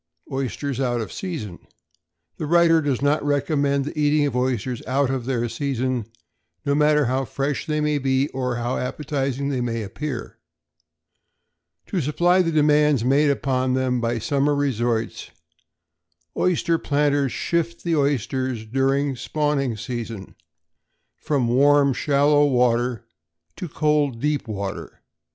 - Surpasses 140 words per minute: No, slow, 135 wpm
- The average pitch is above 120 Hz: Yes, medium, 140 Hz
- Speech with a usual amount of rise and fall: Yes, average, 3.0 semitones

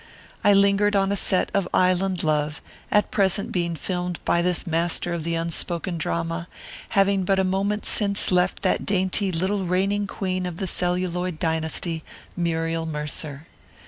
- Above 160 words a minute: No, average, 155 wpm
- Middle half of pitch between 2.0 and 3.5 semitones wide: Yes, narrow, 2.6 semitones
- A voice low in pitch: No, medium, 180 Hz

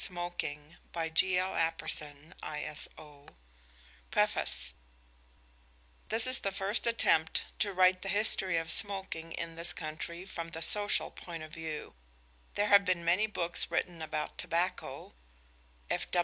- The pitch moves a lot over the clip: No, average, 3.1 semitones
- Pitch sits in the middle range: Yes, medium, 175 Hz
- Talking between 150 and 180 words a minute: No, slow, 135 wpm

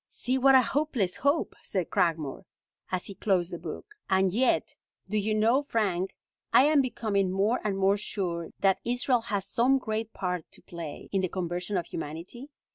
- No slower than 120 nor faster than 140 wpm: No, average, 180 wpm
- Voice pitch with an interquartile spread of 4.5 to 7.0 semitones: Yes, average, 4.9 semitones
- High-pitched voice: Yes, high, 200 Hz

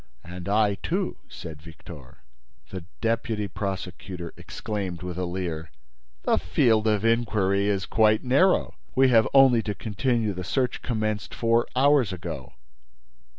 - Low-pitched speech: Yes, low, 105 Hz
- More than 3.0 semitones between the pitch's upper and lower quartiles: Yes, average, 4.2 semitones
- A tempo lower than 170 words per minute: Yes, slow, 135 wpm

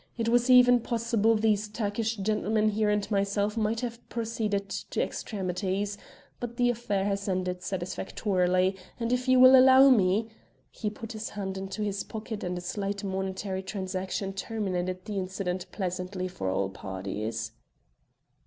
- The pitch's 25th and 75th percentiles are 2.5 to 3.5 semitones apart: Yes, average, 3.1 semitones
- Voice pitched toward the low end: No, high, 200 Hz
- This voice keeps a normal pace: Yes, average, 155 wpm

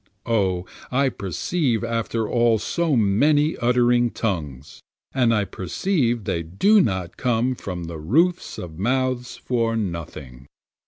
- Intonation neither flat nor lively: No, wide, 5.7 semitones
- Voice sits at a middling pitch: No, low, 115 Hz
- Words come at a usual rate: No, slow, 125 wpm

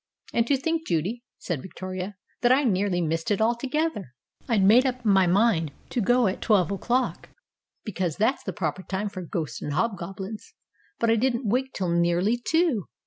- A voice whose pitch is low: No, high, 205 Hz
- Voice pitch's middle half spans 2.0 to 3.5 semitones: No, average, 5.0 semitones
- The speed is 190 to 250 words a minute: No, average, 175 wpm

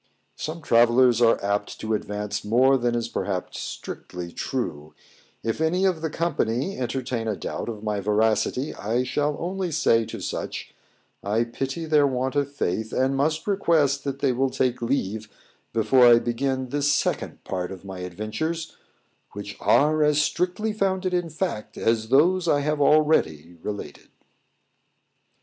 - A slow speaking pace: No, average, 150 wpm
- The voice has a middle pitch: No, low, 130 Hz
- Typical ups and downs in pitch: No, wide, 5.8 semitones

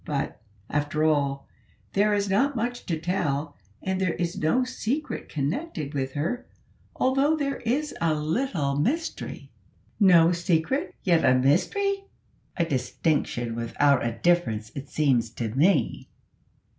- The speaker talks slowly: Yes, slow, 130 wpm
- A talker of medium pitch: Yes, medium, 165 Hz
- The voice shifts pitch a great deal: Yes, wide, 8.3 semitones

